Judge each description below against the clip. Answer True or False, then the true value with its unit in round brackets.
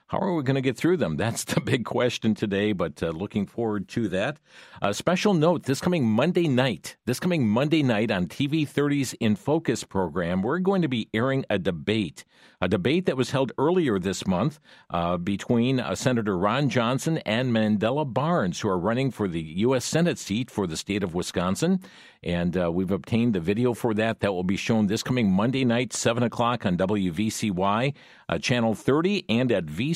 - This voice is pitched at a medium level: False (120 Hz)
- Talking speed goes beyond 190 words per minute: True (200 wpm)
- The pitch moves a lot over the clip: False (5.0 semitones)